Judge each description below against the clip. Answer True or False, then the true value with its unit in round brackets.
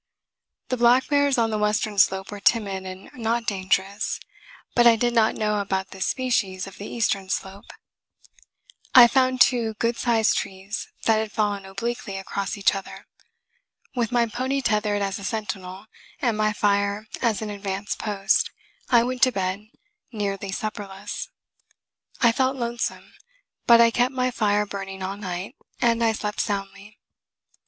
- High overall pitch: True (210 Hz)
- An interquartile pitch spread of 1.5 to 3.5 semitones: True (3.2 semitones)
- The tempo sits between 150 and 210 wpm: True (155 wpm)